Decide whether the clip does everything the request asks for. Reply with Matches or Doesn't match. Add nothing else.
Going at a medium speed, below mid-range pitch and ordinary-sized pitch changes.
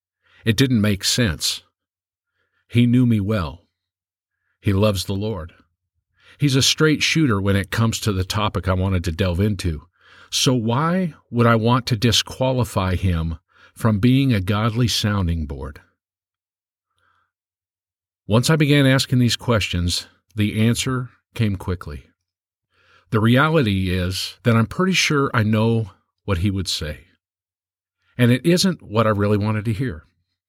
Matches